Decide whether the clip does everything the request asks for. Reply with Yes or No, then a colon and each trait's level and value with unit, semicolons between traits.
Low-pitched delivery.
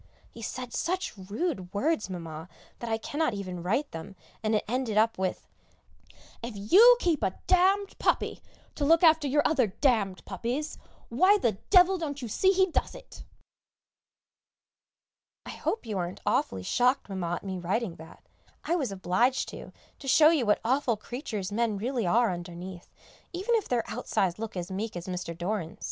No: high, 225 Hz